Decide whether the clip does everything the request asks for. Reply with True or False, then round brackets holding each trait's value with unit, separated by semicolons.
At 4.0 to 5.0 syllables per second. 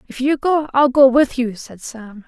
True (4.4 syllables/s)